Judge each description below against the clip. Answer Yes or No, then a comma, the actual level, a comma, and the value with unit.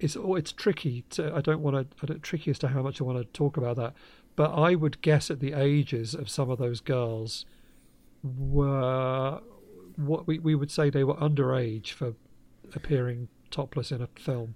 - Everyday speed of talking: Yes, average, 190 wpm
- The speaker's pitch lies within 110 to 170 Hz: Yes, medium, 140 Hz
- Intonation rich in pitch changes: No, average, 3.4 semitones